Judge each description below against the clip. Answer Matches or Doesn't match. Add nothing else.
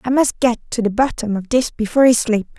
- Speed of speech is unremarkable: Doesn't match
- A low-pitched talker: Doesn't match